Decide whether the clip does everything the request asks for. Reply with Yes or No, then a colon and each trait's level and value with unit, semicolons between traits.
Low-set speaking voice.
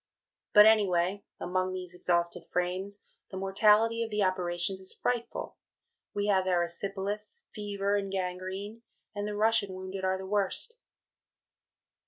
No: high, 195 Hz